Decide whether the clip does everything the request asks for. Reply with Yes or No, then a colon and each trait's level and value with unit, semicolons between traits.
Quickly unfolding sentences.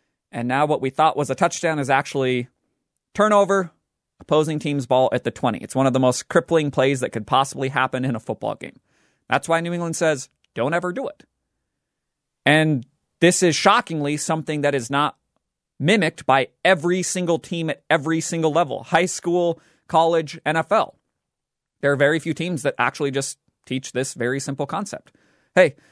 No: average, 175 wpm